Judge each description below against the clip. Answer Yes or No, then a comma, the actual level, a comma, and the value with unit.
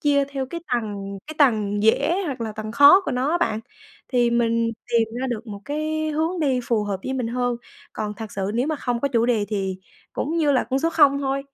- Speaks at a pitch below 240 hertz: No, high, 245 Hz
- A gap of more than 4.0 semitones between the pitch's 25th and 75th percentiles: Yes, average, 4.7 semitones